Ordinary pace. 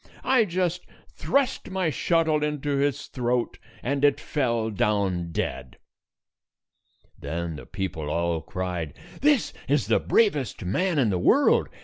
No: slow, 130 wpm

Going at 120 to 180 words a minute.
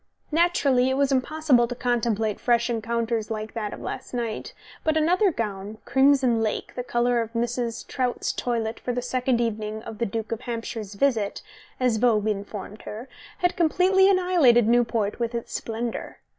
Yes: average, 165 wpm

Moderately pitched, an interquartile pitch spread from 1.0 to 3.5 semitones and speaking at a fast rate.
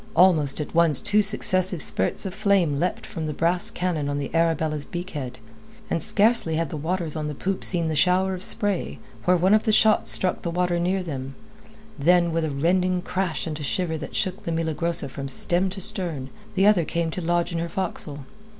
Yes: medium, 170 Hz; average, 2.9 semitones; fast, 210 wpm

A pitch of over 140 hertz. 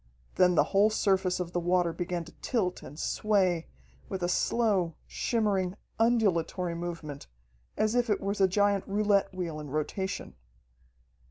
Yes: medium, 185 Hz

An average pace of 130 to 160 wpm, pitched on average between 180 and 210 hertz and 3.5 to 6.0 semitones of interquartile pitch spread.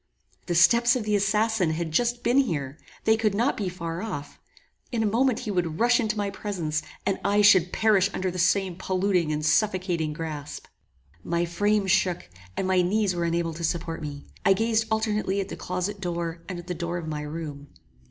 No: average, 200 wpm; medium, 185 Hz; average, 4.1 semitones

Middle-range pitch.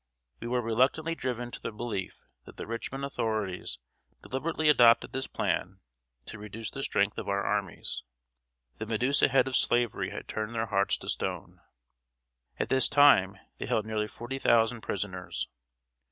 No: low, 115 Hz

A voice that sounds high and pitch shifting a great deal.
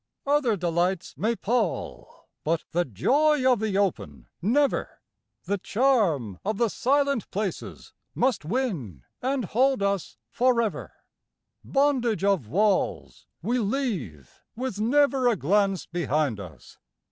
Yes: high, 210 Hz; wide, 6.7 semitones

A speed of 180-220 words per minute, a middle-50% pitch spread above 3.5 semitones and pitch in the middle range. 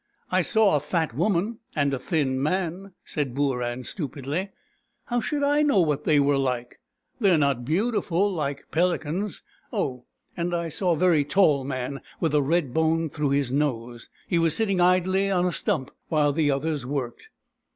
Yes: average, 185 wpm; average, 4.7 semitones; medium, 155 Hz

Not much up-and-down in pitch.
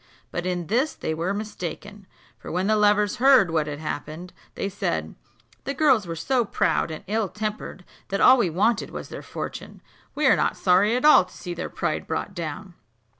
No: average, 4.3 semitones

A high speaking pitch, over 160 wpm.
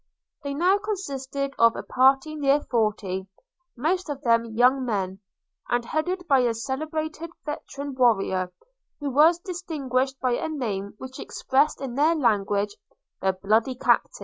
No: very high, 265 Hz; average, 145 wpm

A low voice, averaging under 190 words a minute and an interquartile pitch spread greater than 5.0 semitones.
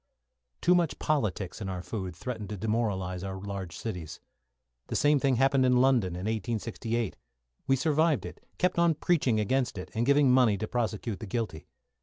Yes: low, 115 Hz; average, 180 wpm; wide, 5.4 semitones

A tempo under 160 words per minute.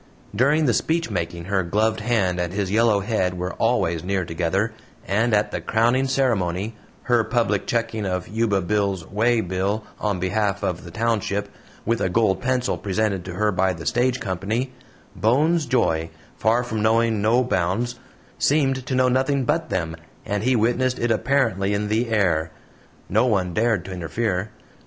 No: average, 165 wpm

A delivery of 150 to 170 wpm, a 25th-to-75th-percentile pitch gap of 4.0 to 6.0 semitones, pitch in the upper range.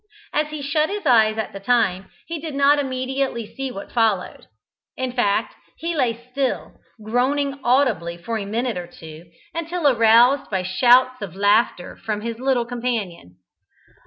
Yes: average, 160 wpm; average, 4.8 semitones; high, 240 Hz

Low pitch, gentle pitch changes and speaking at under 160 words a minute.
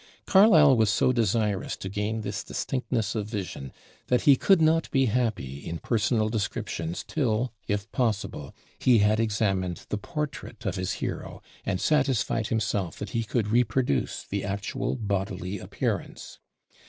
No: low, 110 Hz; average, 3.8 semitones; average, 145 wpm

